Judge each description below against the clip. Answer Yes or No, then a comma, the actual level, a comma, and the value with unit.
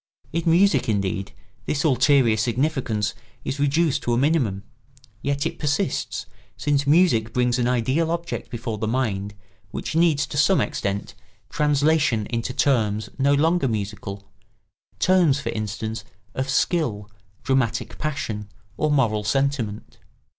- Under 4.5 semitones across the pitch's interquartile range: No, wide, 5.4 semitones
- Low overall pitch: Yes, low, 130 Hz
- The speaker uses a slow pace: Yes, slow, 125 wpm